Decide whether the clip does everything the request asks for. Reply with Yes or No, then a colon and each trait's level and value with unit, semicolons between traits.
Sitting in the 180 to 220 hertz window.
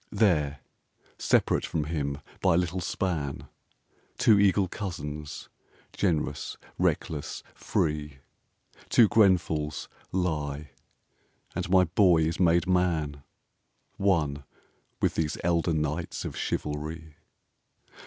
No: very low, 80 Hz